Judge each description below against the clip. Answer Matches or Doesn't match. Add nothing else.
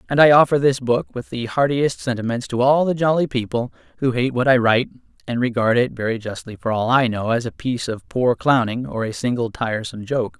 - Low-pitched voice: Matches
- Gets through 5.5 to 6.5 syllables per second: Doesn't match